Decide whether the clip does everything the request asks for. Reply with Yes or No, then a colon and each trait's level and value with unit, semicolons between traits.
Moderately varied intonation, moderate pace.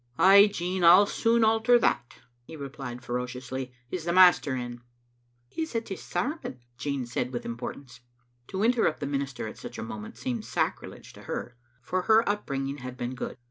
No: wide, 7.6 semitones; average, 190 wpm